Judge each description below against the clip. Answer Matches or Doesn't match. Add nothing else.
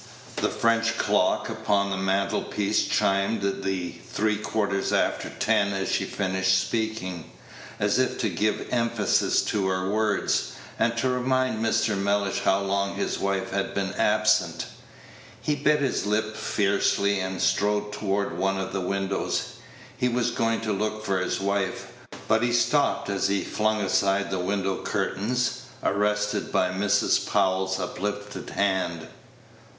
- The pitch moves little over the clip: Matches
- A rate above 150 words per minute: Doesn't match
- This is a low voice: Matches